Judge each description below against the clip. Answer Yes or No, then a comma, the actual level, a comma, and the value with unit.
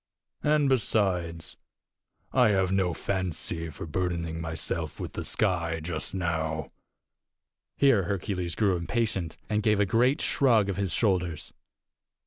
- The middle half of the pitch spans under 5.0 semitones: Yes, average, 4.1 semitones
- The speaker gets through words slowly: Yes, slow, 125 wpm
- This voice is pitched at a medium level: No, very low, 95 Hz